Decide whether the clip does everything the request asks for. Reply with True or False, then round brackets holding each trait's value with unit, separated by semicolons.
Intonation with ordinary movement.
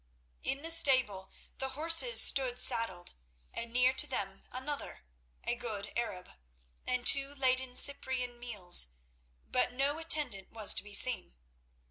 False (5.7 semitones)